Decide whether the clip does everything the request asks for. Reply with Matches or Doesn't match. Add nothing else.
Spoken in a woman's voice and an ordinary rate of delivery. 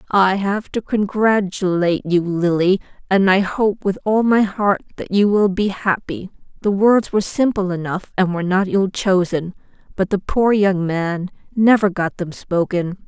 Matches